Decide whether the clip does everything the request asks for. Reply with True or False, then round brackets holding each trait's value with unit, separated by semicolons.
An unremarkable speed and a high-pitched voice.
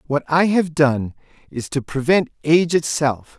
False (160 wpm; 150 Hz)